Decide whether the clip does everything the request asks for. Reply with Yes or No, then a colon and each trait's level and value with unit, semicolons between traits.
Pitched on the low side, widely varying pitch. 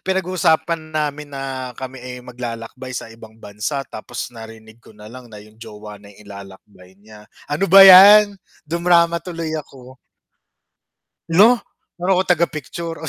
Yes: low, 130 Hz; wide, 7.2 semitones